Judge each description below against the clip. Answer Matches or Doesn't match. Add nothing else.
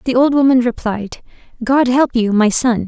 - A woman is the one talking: Matches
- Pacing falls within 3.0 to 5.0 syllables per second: Matches